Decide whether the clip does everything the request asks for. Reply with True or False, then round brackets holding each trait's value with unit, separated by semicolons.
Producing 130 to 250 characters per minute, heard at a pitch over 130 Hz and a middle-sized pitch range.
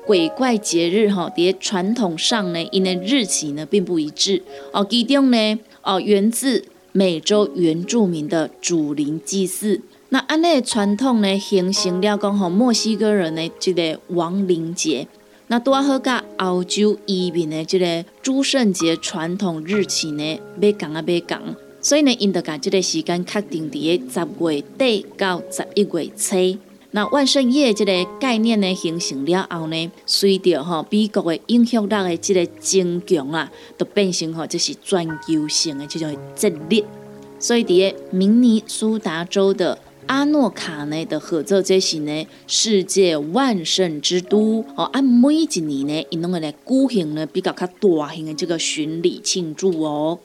True (240 characters per minute; 185 Hz; 4.3 semitones)